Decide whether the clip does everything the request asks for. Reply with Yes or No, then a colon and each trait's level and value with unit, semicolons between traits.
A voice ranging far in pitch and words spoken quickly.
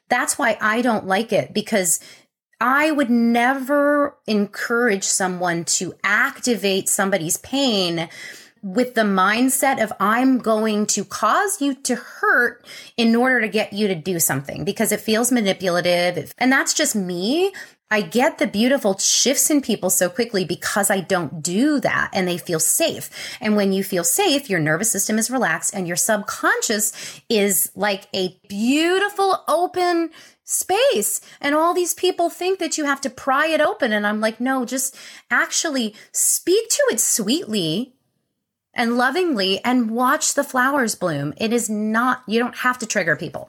No: wide, 5.8 semitones; average, 165 wpm